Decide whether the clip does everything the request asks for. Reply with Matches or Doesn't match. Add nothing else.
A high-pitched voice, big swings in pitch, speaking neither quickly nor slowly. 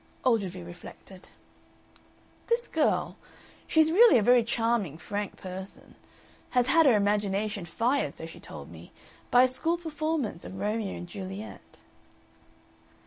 Doesn't match